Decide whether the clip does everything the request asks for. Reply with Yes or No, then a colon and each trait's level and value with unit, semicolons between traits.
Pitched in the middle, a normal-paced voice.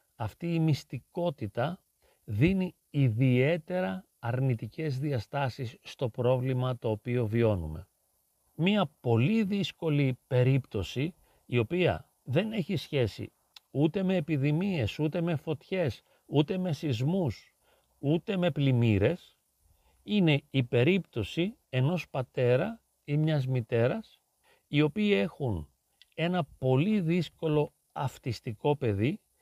No: medium, 145 Hz; slow, 100 wpm